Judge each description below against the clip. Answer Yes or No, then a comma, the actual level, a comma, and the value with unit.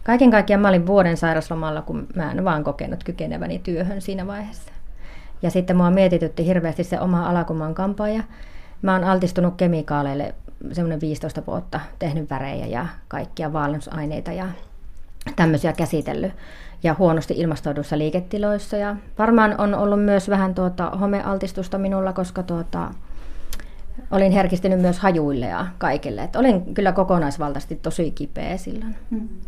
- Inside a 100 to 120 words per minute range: No, average, 145 wpm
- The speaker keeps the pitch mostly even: No, average, 3.7 semitones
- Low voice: No, medium, 180 Hz